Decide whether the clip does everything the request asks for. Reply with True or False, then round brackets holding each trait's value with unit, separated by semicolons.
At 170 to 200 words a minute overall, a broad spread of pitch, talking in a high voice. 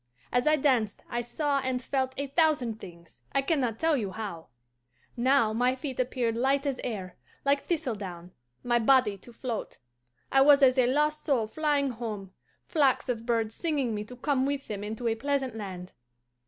False (180 wpm; 4.0 semitones; 250 Hz)